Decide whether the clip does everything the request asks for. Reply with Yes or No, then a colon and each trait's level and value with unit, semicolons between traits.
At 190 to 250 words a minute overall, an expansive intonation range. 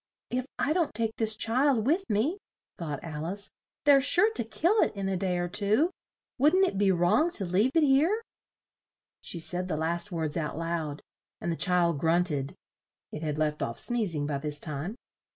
Yes: average, 195 wpm; wide, 8.3 semitones